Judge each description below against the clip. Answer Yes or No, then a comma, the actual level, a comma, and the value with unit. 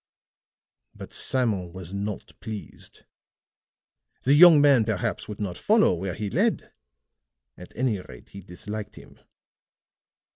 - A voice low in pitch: Yes, low, 105 Hz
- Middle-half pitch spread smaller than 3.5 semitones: No, average, 5.1 semitones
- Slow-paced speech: Yes, slow, 120 wpm